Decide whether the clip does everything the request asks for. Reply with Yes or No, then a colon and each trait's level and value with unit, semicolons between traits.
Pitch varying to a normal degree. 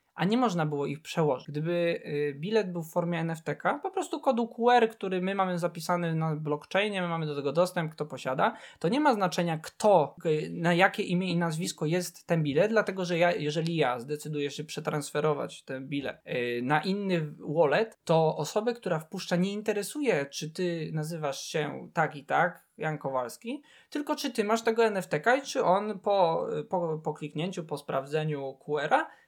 Yes: average, 4.6 semitones